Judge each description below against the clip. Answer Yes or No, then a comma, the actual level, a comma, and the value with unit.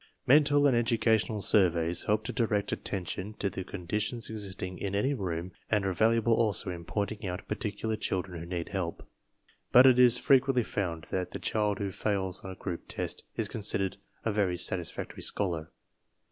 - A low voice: Yes, low, 100 Hz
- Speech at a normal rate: Yes, average, 175 wpm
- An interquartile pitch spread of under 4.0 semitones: Yes, average, 3.4 semitones